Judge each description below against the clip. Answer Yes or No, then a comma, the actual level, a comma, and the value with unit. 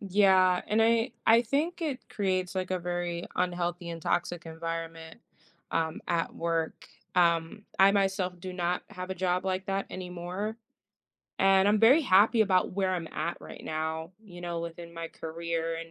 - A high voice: No, medium, 180 Hz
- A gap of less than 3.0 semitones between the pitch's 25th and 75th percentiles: Yes, narrow, 2.5 semitones